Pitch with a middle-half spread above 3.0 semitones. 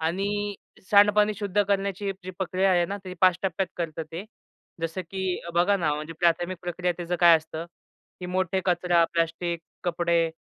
No: narrow, 2.4 semitones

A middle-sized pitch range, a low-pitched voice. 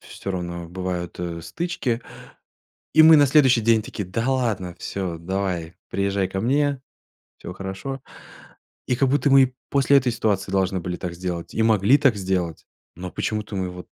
No: wide, 6.1 semitones; low, 100 Hz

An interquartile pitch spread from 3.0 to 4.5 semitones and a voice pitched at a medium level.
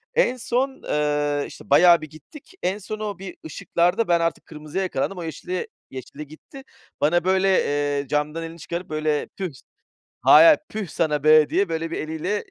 Yes: average, 4.2 semitones; medium, 165 Hz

